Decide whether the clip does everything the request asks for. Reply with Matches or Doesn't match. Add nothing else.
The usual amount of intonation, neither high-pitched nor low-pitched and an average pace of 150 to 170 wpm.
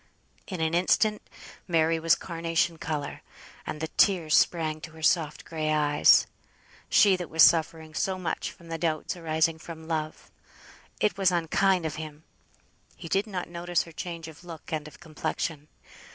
Doesn't match